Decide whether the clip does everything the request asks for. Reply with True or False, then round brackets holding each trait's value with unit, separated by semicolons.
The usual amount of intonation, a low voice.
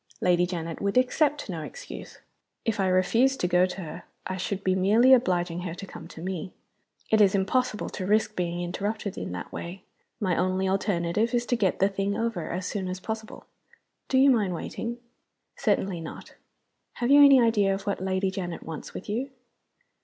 False (3.7 semitones; 195 Hz)